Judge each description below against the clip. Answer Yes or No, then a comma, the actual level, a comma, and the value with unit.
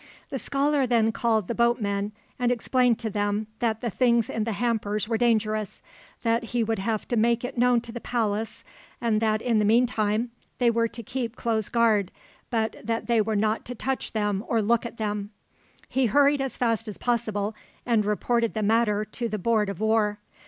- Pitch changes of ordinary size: No, narrow, 1.9 semitones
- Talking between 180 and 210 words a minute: Yes, average, 195 wpm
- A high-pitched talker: Yes, high, 225 Hz